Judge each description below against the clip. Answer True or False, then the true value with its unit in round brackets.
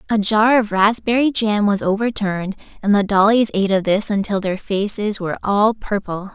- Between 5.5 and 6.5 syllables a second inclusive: False (5.2 syllables/s)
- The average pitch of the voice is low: False (205 Hz)